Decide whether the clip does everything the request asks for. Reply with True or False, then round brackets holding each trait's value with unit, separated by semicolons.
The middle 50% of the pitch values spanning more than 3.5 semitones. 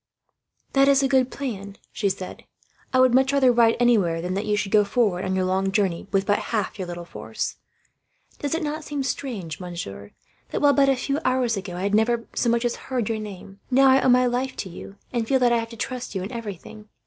True (4.9 semitones)